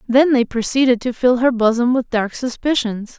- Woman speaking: Yes, female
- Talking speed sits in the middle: Yes, average, 190 wpm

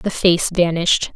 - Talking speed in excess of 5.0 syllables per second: No, 4.8 syllables/s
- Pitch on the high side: No, medium, 175 Hz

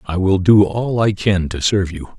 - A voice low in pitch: Yes, very low, 95 Hz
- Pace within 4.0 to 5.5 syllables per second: Yes, 5.0 syllables/s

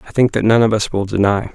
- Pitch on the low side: Yes, low, 110 Hz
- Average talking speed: No, fast, 310 wpm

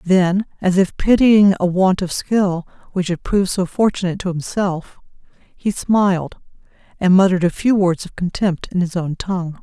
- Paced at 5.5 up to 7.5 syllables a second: No, 4.9 syllables/s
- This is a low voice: No, medium, 185 Hz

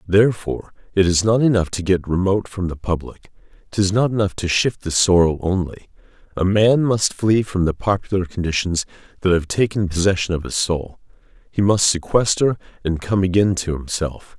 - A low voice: Yes, very low, 95 Hz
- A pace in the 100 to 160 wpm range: No, average, 175 wpm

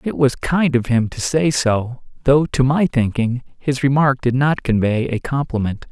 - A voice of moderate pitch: No, low, 130 Hz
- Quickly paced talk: No, average, 195 wpm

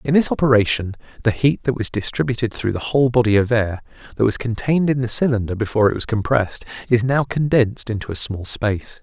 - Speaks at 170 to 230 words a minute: Yes, fast, 205 wpm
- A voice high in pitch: No, low, 115 Hz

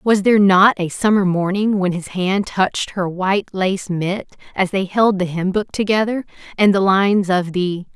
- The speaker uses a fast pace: No, average, 195 wpm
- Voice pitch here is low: No, high, 195 Hz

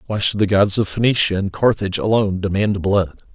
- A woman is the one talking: No, male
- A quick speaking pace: No, average, 195 wpm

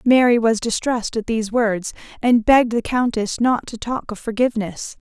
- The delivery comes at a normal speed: Yes, average, 175 wpm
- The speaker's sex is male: No, female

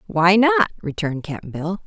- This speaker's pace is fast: No, average, 160 wpm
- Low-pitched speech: No, medium, 185 Hz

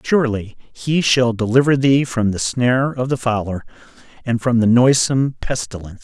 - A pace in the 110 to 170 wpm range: Yes, average, 160 wpm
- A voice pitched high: No, low, 120 Hz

